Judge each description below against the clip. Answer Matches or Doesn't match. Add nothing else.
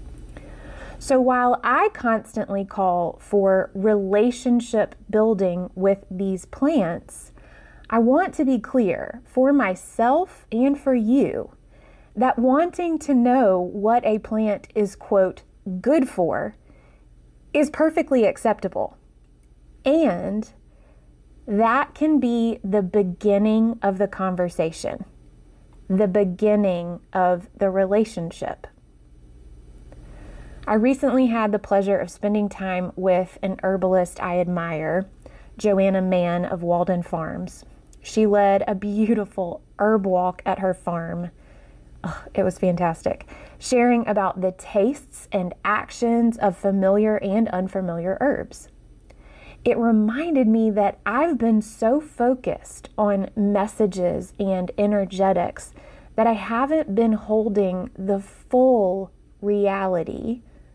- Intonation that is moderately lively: Matches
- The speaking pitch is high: Matches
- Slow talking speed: Matches